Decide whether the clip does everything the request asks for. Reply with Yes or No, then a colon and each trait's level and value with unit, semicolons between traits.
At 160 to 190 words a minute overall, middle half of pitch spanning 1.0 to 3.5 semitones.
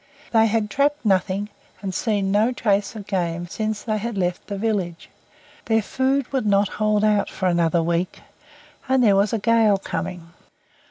Yes: average, 170 wpm; average, 2.9 semitones